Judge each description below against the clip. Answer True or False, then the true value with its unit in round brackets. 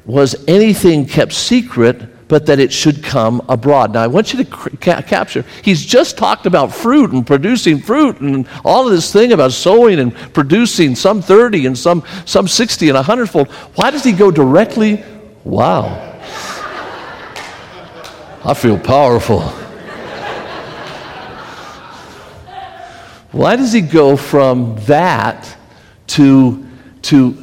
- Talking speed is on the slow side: True (130 wpm)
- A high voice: False (160 Hz)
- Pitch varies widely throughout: True (8.1 semitones)